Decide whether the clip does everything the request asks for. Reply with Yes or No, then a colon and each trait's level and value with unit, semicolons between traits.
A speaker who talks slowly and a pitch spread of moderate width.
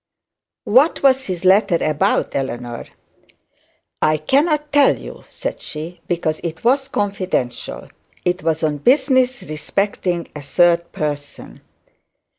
No: slow, 115 wpm; wide, 8.8 semitones